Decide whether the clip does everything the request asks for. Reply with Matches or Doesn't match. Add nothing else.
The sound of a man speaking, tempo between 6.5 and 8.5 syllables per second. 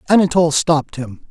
Matches